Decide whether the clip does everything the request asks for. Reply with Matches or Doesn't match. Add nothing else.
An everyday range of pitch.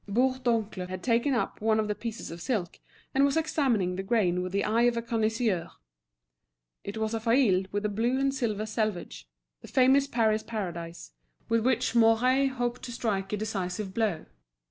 Matches